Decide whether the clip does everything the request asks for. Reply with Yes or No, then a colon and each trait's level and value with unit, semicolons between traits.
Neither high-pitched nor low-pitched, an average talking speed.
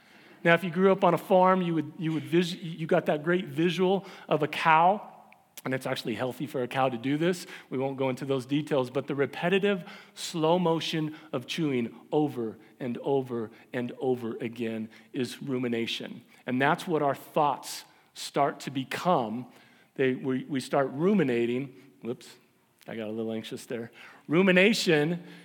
Yes: medium, 150 Hz; average, 170 wpm